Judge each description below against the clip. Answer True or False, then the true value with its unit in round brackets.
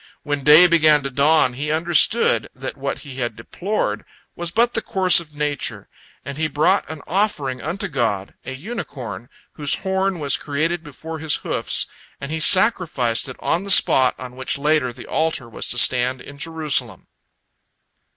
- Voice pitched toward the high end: False (150 Hz)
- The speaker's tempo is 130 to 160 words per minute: False (170 wpm)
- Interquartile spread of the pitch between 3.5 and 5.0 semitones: True (4.5 semitones)